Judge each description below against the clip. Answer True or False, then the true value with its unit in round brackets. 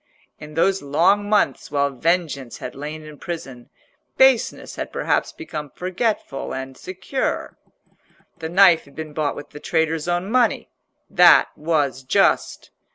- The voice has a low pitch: False (160 Hz)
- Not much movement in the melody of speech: False (4.6 semitones)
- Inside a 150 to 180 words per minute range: False (140 wpm)